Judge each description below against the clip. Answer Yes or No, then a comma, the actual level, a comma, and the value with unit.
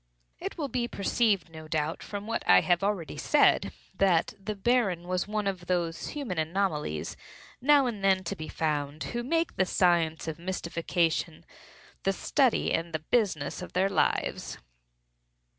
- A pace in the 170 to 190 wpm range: No, average, 160 wpm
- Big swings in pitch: No, average, 4.4 semitones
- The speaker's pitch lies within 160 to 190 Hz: Yes, medium, 185 Hz